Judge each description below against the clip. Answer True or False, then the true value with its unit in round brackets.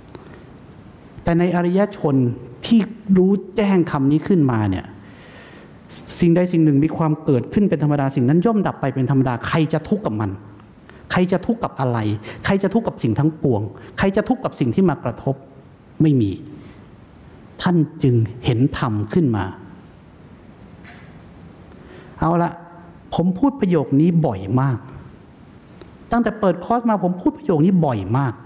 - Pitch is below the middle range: False (155 Hz)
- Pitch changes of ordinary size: False (6.9 semitones)